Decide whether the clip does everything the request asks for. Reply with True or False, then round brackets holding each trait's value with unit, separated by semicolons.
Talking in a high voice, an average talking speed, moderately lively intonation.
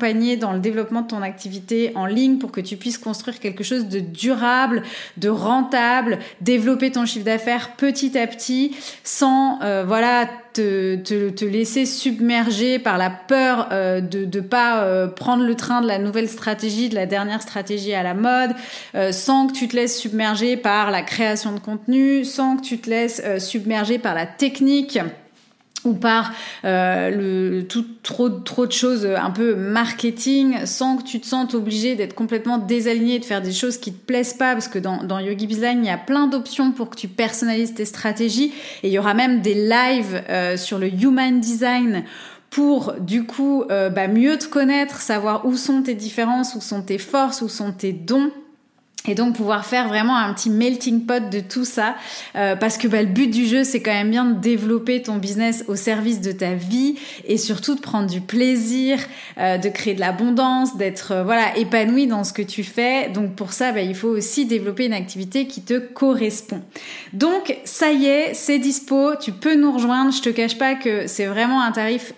True (230 Hz; 205 wpm; 3.5 semitones)